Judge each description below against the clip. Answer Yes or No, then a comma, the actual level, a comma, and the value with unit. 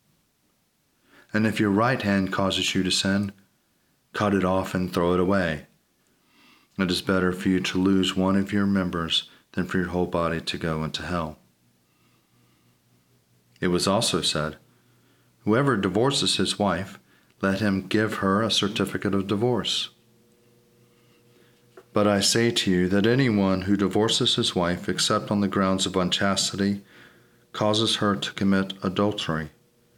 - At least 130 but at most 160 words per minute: Yes, average, 150 wpm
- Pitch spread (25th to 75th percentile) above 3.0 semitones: No, narrow, 2.6 semitones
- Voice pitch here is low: Yes, very low, 95 Hz